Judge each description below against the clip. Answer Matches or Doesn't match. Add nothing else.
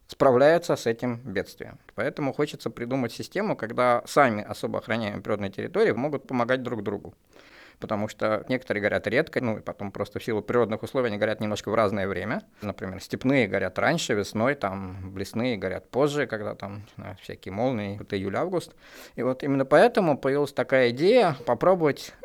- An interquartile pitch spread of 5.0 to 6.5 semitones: Doesn't match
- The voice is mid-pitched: Doesn't match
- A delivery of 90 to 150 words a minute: Doesn't match